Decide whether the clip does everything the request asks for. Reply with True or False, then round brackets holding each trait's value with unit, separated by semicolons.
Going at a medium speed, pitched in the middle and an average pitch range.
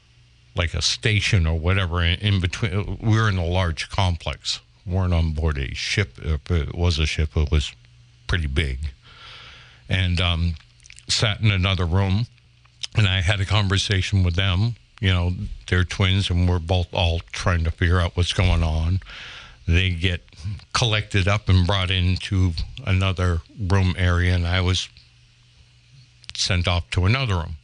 False (160 wpm; 95 Hz; 3.2 semitones)